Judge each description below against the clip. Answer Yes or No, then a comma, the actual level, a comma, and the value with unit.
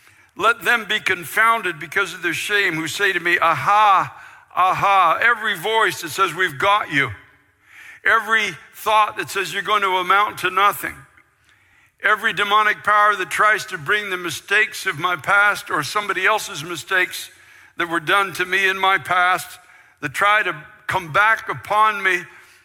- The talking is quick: No, average, 165 wpm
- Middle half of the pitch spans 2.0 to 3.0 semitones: Yes, average, 2.7 semitones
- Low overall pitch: No, high, 195 Hz